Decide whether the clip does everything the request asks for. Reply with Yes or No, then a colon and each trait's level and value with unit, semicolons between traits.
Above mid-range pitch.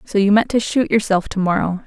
Yes: high, 205 Hz